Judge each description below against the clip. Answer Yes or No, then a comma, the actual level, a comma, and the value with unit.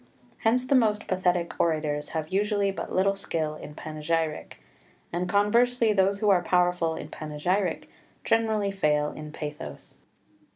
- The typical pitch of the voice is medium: Yes, medium, 180 Hz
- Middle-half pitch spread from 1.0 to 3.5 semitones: No, average, 4.8 semitones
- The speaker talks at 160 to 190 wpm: No, slow, 135 wpm